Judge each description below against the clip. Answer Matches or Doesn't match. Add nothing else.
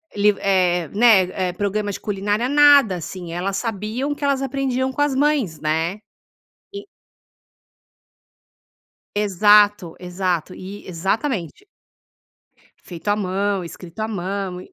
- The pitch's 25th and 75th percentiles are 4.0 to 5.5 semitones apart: Matches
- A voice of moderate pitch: Doesn't match